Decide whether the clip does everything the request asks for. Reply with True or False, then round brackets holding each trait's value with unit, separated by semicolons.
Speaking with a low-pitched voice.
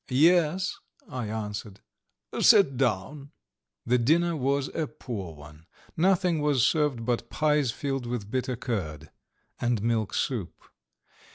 True (125 Hz)